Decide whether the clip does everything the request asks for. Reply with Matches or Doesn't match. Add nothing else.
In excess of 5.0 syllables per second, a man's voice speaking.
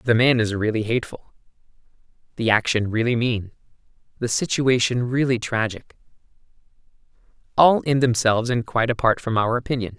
Matches